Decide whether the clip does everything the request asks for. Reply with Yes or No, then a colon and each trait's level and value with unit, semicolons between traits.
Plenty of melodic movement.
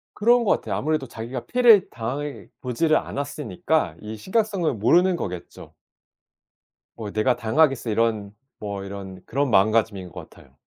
Yes: wide, 6.8 semitones